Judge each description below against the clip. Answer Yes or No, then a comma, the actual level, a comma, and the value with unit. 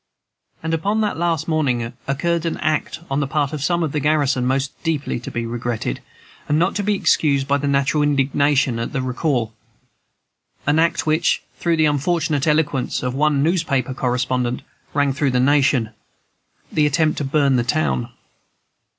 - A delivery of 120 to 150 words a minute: No, average, 170 wpm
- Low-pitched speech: No, medium, 145 Hz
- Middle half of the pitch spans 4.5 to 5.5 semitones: No, average, 3.3 semitones